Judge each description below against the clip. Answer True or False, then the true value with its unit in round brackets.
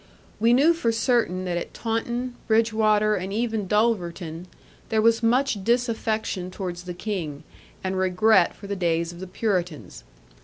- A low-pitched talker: False (210 Hz)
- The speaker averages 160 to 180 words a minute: False (150 wpm)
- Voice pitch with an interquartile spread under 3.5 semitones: False (4.0 semitones)